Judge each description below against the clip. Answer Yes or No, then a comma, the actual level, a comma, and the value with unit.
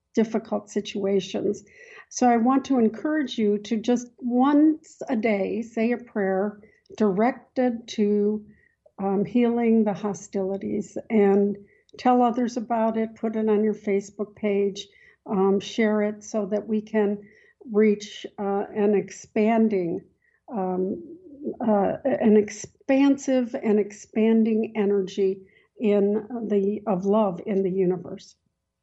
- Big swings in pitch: No, average, 2.8 semitones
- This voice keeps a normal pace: No, slow, 120 wpm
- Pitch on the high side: Yes, high, 215 Hz